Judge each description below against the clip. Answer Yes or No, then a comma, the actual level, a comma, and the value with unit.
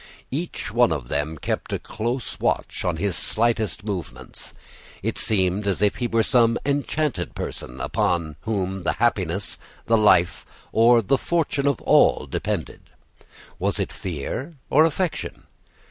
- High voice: No, low, 110 Hz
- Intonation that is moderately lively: No, wide, 5.7 semitones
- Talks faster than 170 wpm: No, average, 145 wpm